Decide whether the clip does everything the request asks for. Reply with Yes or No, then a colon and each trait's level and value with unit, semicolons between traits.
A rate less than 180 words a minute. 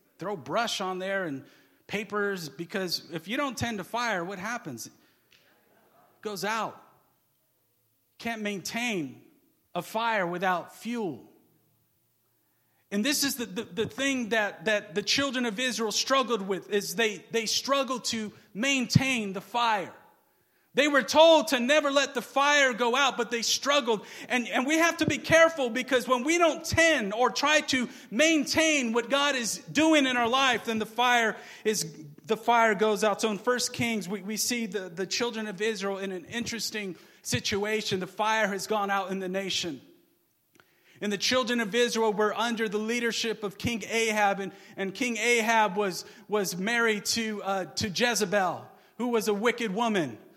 Yes: average, 170 wpm